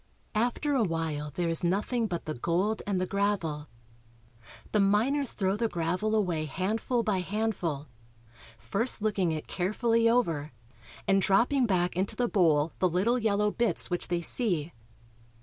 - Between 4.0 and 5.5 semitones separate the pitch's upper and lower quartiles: Yes, average, 4.7 semitones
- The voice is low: No, high, 195 Hz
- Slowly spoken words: No, average, 150 wpm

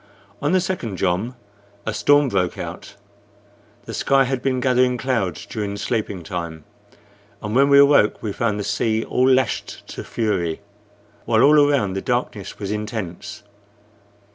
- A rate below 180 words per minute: Yes, average, 150 wpm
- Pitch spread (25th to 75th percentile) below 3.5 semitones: No, average, 4.8 semitones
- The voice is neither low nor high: No, low, 115 Hz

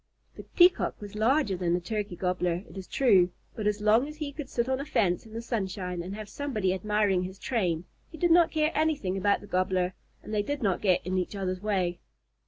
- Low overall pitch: No, high, 205 Hz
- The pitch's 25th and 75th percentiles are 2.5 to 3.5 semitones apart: No, average, 5.2 semitones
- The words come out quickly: Yes, fast, 225 wpm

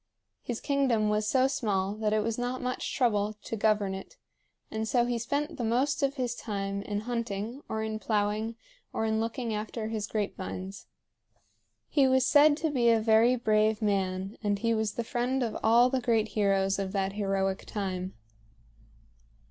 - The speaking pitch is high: Yes, high, 220 Hz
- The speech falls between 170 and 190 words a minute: Yes, average, 180 wpm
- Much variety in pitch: No, average, 2.9 semitones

